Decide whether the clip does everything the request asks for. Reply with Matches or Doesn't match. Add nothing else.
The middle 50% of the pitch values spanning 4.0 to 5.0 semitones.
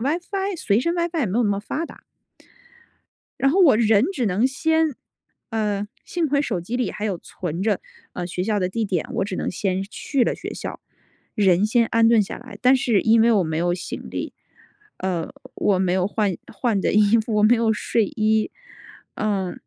Matches